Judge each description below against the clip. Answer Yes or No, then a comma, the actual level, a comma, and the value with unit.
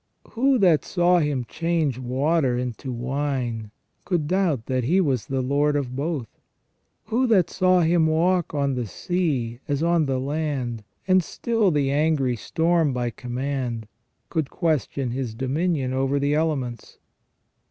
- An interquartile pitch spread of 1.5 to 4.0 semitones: No, average, 4.7 semitones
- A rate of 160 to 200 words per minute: No, average, 140 wpm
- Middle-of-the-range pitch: Yes, medium, 145 Hz